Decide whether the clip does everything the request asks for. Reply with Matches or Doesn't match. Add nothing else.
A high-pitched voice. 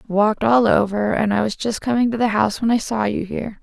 Matches